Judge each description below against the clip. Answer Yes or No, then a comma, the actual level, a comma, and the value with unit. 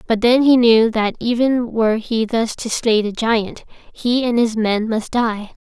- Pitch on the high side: Yes, high, 230 Hz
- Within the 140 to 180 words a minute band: No, fast, 205 wpm